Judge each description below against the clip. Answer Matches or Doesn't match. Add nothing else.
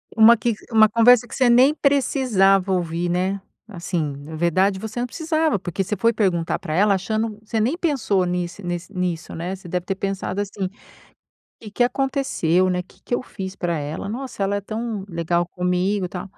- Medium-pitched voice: Doesn't match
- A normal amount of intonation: Matches